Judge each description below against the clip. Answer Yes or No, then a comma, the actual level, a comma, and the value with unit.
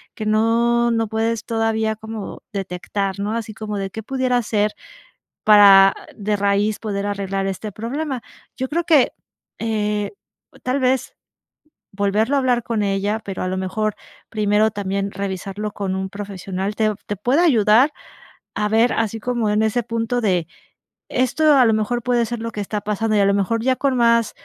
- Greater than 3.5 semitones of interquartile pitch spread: No, narrow, 2.6 semitones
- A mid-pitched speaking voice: No, high, 215 Hz